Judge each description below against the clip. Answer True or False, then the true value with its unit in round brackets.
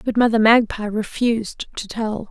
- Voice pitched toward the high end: True (220 Hz)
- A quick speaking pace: False (155 wpm)